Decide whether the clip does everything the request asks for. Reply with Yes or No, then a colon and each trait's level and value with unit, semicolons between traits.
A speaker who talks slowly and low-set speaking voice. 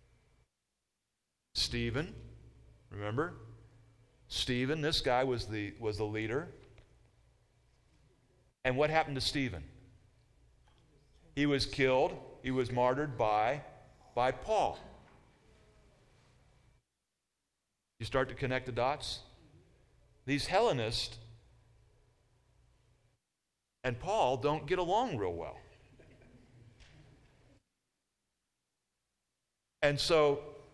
Yes: slow, 80 wpm; low, 125 Hz